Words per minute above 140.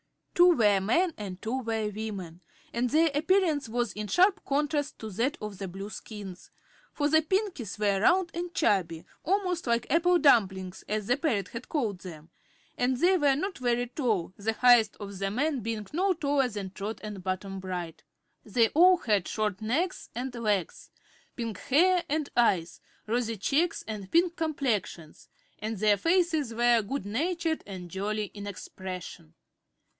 Yes: average, 160 wpm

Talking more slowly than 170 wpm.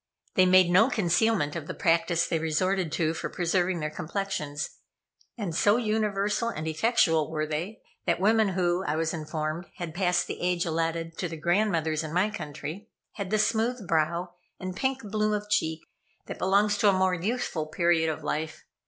No: average, 180 wpm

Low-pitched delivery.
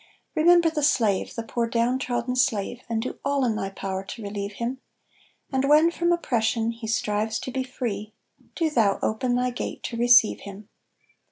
No: high, 235 Hz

